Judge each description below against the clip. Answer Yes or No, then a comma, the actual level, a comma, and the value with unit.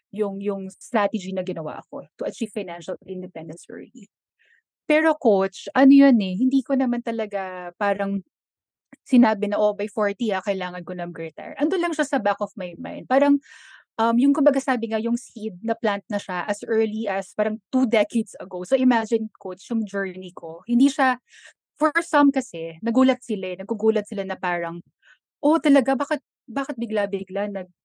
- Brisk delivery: No, average, 180 wpm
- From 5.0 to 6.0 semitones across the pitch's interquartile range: Yes, average, 5.3 semitones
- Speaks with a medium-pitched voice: No, high, 215 Hz